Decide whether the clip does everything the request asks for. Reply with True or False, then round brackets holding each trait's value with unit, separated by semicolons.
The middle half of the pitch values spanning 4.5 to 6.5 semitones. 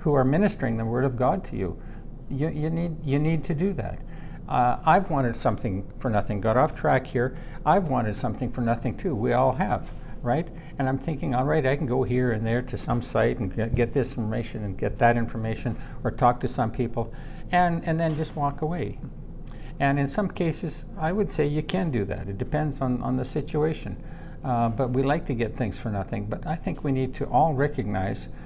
True (4.8 semitones)